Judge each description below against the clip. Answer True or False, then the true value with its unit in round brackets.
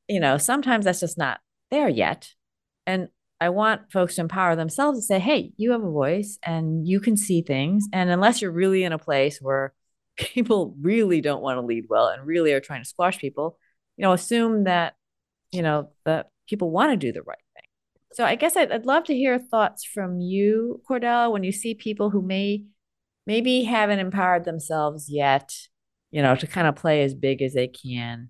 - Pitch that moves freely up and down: True (6.2 semitones)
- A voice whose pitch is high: False (180 Hz)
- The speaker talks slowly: False (205 wpm)